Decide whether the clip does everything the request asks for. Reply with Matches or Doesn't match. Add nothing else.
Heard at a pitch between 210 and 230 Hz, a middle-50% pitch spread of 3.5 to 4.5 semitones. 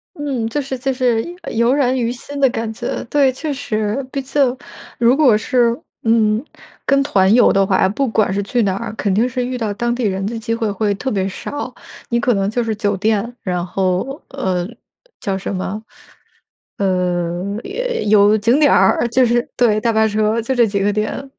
Matches